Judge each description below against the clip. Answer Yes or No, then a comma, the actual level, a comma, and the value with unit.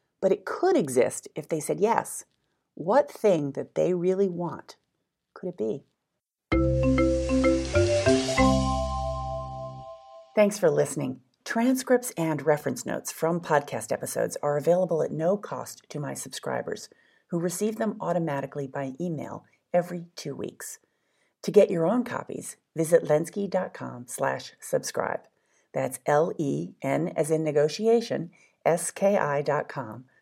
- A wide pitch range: Yes, wide, 6.2 semitones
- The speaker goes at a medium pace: No, slow, 120 wpm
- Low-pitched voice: No, medium, 150 Hz